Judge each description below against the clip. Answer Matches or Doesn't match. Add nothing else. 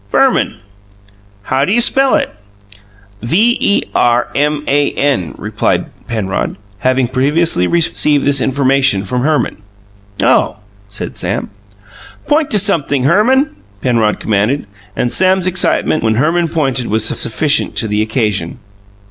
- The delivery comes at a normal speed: Doesn't match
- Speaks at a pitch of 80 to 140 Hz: Matches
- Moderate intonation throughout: Doesn't match